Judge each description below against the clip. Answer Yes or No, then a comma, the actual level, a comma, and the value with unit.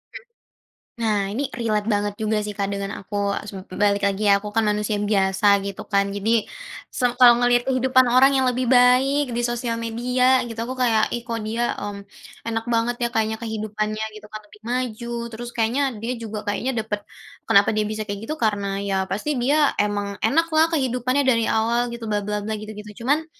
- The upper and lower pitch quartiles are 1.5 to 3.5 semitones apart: Yes, average, 2.9 semitones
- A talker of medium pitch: No, high, 225 Hz